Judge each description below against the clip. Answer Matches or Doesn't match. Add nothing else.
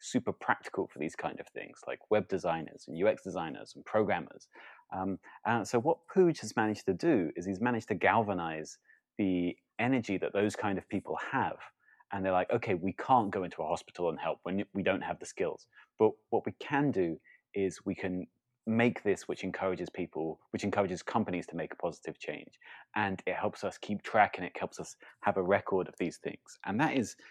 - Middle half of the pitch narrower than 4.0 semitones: Matches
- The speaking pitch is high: Doesn't match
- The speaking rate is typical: Doesn't match